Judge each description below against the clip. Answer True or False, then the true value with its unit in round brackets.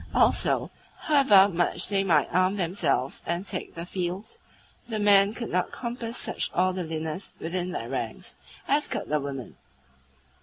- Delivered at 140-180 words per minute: True (145 wpm)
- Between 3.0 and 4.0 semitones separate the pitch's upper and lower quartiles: True (3.3 semitones)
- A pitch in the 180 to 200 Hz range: True (185 Hz)